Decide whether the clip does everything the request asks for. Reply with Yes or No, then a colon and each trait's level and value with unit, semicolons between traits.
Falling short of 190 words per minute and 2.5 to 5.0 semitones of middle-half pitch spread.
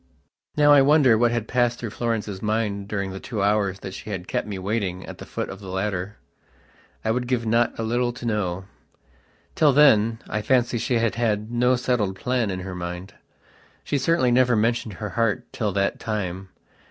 No: average, 195 wpm; average, 3.6 semitones